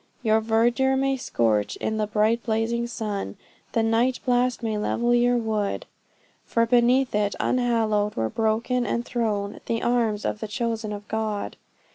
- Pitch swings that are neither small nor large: No, narrow, 2.3 semitones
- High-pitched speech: Yes, high, 225 Hz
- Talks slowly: No, average, 155 wpm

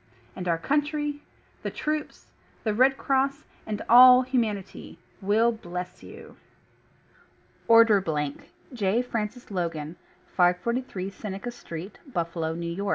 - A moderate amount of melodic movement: No, wide, 5.8 semitones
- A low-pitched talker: No, high, 210 Hz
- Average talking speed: No, slow, 115 wpm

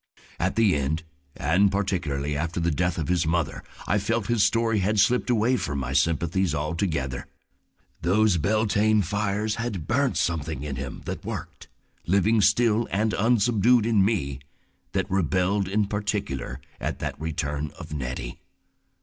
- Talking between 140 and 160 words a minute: Yes, average, 150 wpm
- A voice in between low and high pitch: No, very low, 95 Hz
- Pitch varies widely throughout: Yes, wide, 5.7 semitones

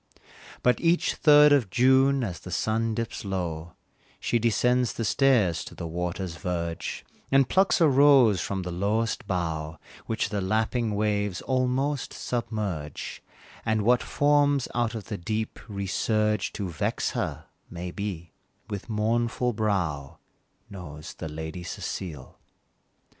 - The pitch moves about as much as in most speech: No, wide, 5.7 semitones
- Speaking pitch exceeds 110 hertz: No, low, 105 Hz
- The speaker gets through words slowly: Yes, slow, 130 wpm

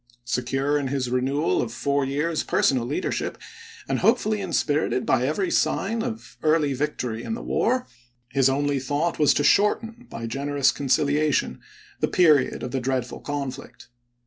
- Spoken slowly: No, average, 155 wpm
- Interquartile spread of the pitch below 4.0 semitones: Yes, average, 3.1 semitones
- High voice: No, medium, 145 Hz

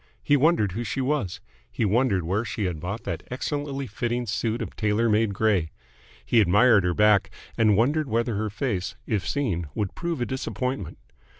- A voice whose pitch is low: Yes, low, 110 Hz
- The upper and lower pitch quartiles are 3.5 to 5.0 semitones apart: Yes, average, 4.1 semitones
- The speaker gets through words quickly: No, average, 180 wpm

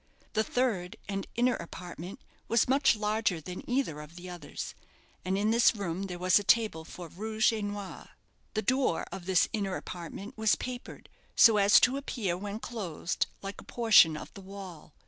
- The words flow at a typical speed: Yes, average, 180 wpm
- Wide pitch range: No, average, 3.8 semitones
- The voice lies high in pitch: Yes, high, 200 Hz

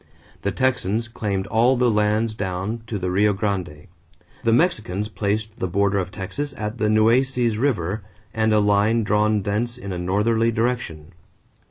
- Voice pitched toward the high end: No, low, 105 Hz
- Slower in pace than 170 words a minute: Yes, average, 160 wpm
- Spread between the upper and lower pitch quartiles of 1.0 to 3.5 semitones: Yes, narrow, 2.6 semitones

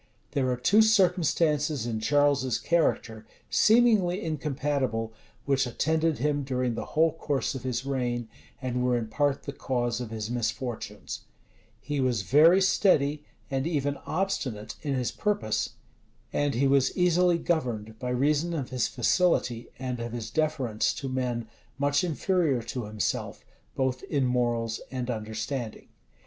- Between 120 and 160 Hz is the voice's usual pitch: Yes, low, 135 Hz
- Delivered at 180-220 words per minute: No, average, 145 wpm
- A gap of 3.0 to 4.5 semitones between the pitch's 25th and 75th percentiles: Yes, average, 4.1 semitones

